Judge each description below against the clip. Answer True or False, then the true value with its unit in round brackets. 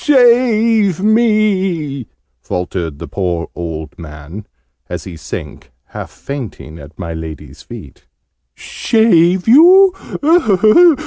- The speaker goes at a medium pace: False (100 wpm)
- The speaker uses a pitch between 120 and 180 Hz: True (140 Hz)